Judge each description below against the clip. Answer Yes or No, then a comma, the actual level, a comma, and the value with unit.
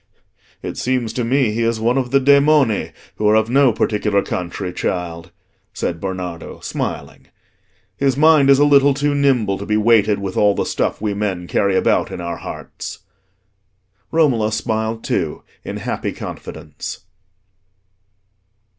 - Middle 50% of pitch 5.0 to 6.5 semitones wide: Yes, average, 5.3 semitones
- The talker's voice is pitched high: No, low, 110 Hz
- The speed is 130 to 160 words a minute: Yes, average, 150 wpm